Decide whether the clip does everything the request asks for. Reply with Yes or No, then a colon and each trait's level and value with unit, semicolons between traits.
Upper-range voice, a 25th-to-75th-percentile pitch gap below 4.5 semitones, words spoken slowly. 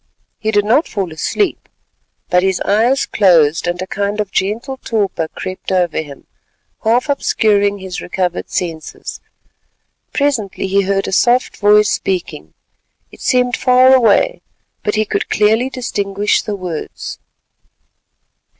Yes: high, 205 Hz; average, 4.1 semitones; slow, 130 wpm